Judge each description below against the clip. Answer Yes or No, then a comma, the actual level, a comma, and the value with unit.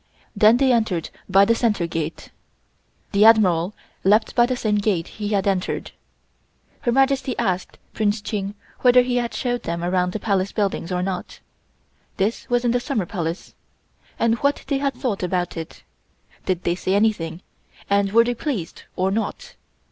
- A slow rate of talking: No, average, 170 wpm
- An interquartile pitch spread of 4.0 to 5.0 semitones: Yes, average, 4.6 semitones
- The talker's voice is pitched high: Yes, high, 205 Hz